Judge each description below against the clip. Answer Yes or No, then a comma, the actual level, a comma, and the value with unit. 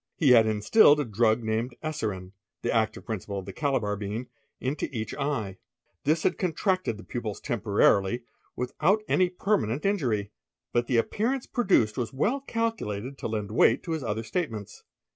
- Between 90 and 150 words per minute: No, average, 160 wpm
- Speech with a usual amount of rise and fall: No, wide, 6.5 semitones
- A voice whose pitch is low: Yes, low, 120 Hz